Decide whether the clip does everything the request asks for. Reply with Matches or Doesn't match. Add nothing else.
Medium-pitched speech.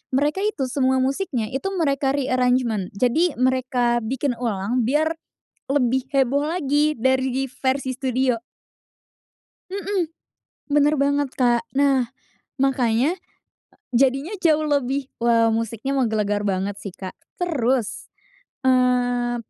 Doesn't match